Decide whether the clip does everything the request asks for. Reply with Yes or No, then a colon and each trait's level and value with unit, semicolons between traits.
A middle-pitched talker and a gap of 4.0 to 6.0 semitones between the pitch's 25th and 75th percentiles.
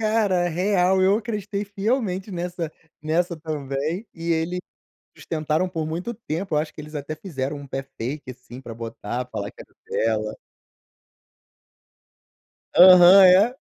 Yes: medium, 170 Hz; average, 4.6 semitones